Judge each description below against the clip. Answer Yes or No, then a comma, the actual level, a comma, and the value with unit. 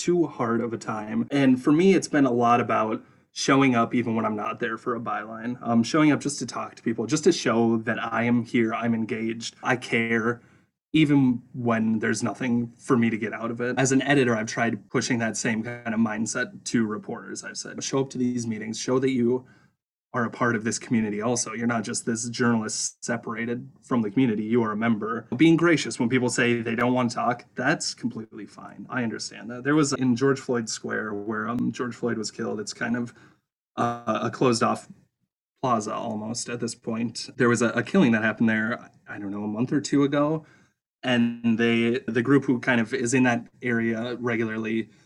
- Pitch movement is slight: Yes, narrow, 2.0 semitones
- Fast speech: Yes, fast, 215 wpm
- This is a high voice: No, low, 120 Hz